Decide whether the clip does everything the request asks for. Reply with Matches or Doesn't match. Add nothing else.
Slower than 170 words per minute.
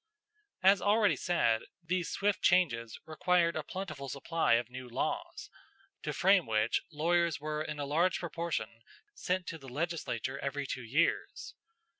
Matches